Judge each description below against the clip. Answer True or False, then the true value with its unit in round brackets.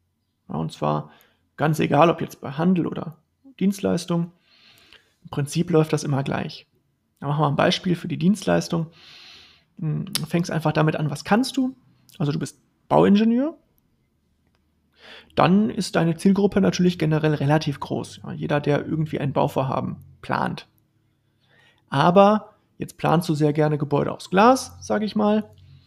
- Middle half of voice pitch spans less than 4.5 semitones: False (4.8 semitones)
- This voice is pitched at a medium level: True (160 Hz)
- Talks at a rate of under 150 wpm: True (140 wpm)